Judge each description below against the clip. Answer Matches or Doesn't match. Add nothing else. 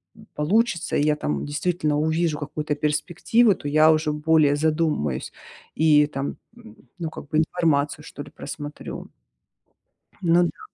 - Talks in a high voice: Doesn't match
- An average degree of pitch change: Doesn't match